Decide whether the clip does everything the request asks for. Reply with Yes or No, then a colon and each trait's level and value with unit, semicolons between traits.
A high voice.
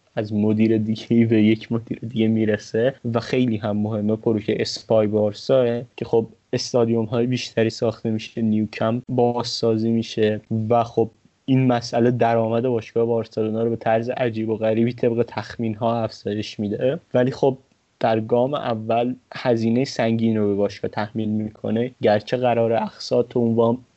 No: low, 115 Hz